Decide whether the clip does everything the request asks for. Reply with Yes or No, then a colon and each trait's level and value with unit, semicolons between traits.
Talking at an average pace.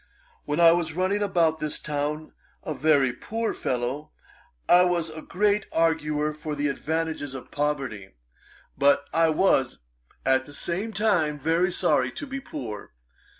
Yes: average, 150 wpm